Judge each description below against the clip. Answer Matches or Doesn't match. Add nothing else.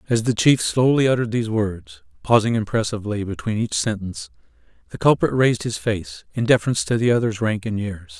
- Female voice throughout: Doesn't match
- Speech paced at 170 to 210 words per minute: Matches